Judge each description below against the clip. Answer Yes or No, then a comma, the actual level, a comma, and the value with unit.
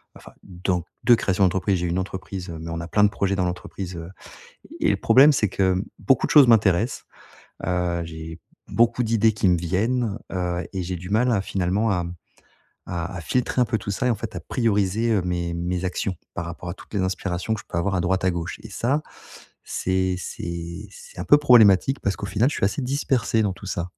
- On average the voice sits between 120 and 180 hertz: No, very low, 95 Hz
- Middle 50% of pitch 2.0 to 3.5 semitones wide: No, average, 3.9 semitones